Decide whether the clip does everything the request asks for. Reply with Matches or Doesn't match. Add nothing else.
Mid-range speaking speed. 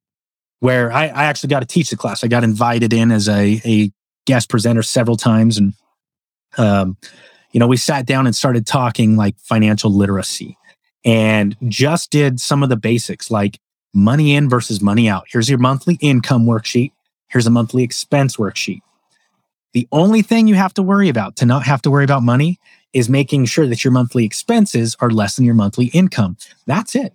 Matches